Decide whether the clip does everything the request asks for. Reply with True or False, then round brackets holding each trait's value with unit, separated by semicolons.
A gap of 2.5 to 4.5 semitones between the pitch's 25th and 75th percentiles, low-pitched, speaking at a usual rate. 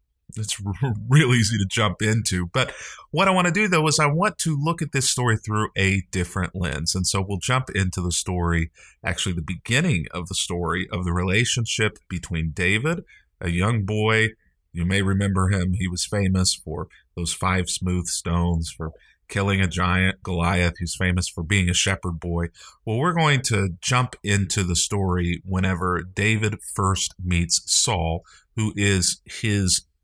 True (3.6 semitones; 95 Hz; 170 wpm)